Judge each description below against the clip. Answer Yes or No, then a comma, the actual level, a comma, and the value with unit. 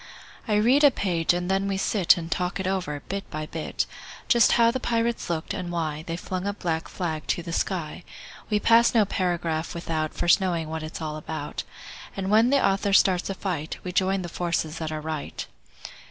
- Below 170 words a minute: No, fast, 205 wpm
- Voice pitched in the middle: Yes, medium, 180 Hz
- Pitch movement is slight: No, average, 3.6 semitones